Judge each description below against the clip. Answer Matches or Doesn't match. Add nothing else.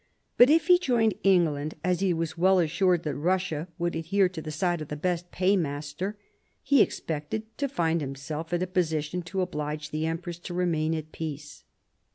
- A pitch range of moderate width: Matches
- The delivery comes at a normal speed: Matches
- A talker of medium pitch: Matches